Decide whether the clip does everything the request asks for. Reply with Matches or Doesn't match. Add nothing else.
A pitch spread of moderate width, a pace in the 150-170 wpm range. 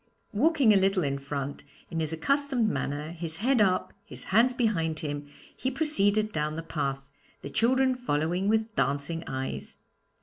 Doesn't match